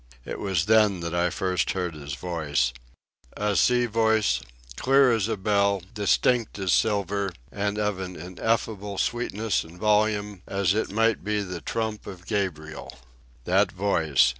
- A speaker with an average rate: Yes, average, 145 wpm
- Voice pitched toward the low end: Yes, low, 100 Hz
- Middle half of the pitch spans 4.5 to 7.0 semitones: No, average, 3.2 semitones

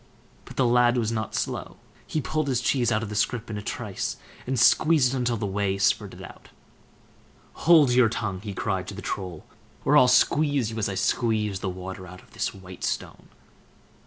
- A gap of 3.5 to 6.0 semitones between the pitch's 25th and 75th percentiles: Yes, average, 4.2 semitones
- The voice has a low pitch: Yes, low, 110 Hz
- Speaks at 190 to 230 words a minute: Yes, average, 200 wpm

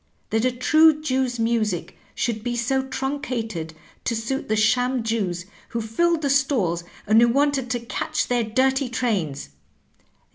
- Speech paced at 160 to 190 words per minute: No, average, 150 wpm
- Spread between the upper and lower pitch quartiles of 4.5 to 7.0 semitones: No, average, 3.3 semitones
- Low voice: No, high, 240 Hz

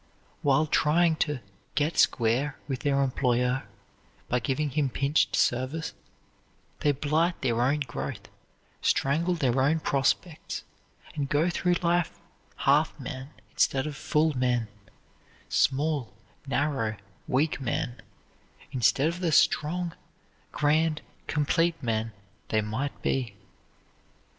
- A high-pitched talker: No, medium, 140 Hz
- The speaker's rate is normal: No, slow, 115 wpm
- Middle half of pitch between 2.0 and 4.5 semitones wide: Yes, average, 3.6 semitones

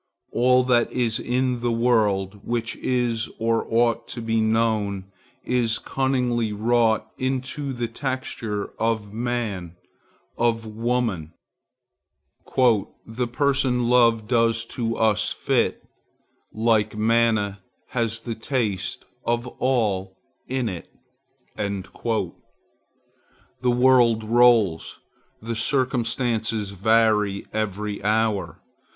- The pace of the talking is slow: Yes, slow, 95 wpm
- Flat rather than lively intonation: Yes, narrow, 2.3 semitones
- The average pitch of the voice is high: No, low, 115 Hz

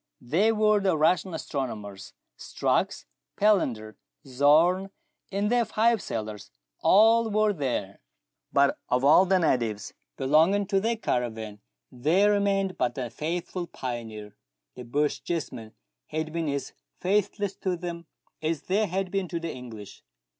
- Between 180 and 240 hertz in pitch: No, medium, 165 Hz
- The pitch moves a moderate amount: No, wide, 7.8 semitones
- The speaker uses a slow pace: Yes, slow, 130 wpm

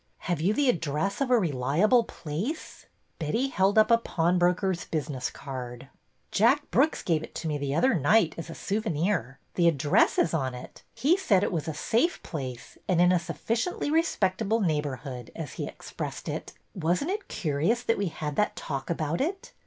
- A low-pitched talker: No, medium, 175 Hz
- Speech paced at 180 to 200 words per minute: Yes, average, 190 wpm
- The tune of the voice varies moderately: No, wide, 7.1 semitones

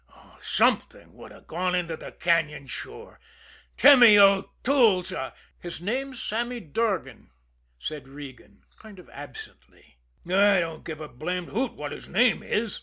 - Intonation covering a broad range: Yes, wide, 6.0 semitones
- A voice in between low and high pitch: Yes, medium, 180 Hz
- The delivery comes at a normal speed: Yes, average, 145 wpm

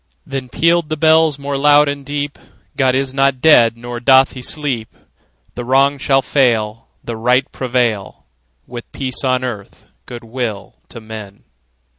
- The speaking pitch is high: No, low, 130 Hz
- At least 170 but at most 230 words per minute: No, average, 155 wpm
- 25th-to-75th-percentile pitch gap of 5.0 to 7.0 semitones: No, average, 3.0 semitones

